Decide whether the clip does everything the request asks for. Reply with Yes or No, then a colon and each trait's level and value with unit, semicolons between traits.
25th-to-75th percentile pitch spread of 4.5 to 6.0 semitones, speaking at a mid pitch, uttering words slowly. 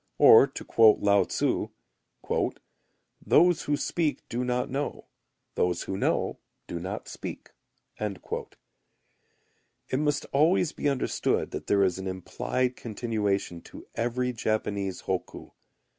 No: wide, 5.5 semitones; low, 115 Hz; slow, 120 wpm